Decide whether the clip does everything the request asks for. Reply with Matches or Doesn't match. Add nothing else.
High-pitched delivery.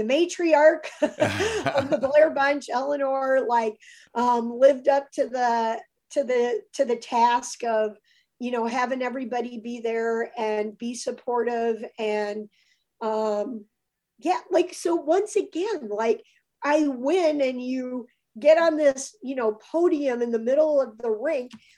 Matches